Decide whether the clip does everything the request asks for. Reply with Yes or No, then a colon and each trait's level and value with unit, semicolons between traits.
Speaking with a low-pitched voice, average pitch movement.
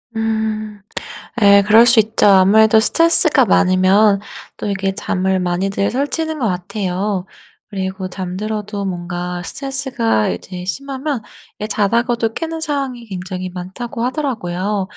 No: high, 205 Hz; average, 4.1 semitones